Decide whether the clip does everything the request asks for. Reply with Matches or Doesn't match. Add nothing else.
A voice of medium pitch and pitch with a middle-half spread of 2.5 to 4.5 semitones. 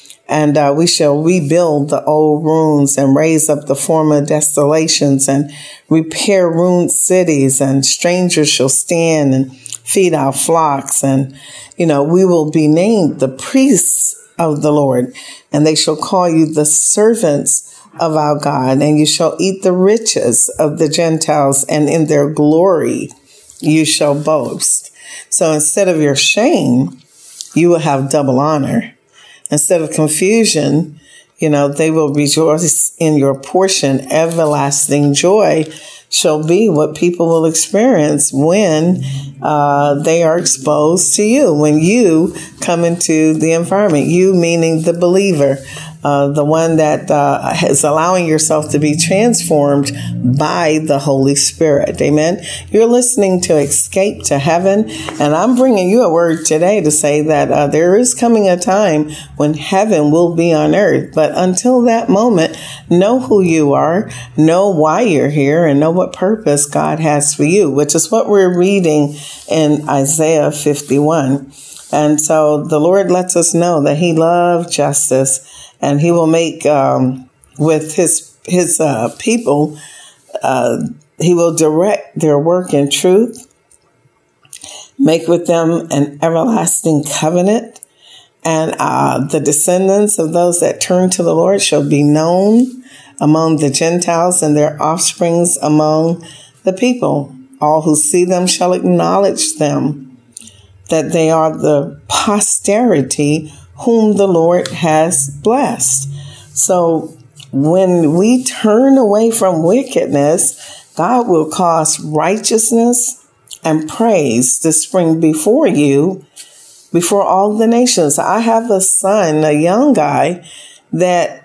Matches